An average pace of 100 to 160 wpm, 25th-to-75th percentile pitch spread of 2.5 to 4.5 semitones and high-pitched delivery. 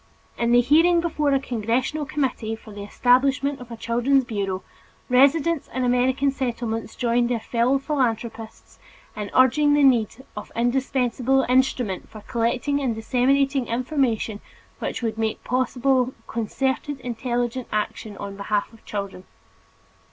Yes: slow, 135 wpm; average, 3.0 semitones; high, 245 Hz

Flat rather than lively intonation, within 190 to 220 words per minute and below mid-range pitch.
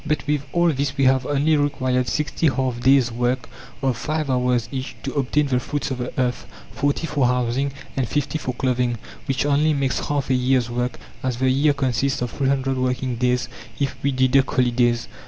Yes: narrow, 2.0 semitones; average, 195 wpm; low, 130 Hz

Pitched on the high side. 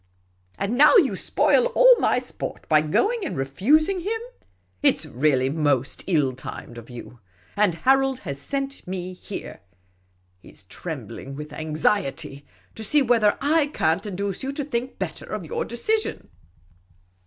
Yes: high, 200 Hz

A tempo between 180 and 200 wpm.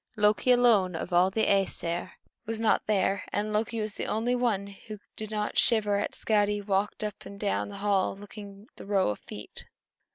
Yes: average, 195 wpm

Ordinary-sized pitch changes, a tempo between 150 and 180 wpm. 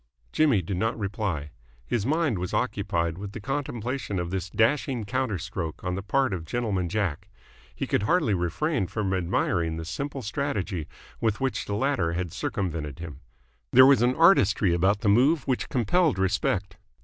No: wide, 6.3 semitones; average, 170 wpm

